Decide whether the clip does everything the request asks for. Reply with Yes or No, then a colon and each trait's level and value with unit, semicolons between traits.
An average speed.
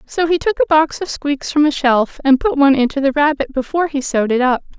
No: fast, 265 wpm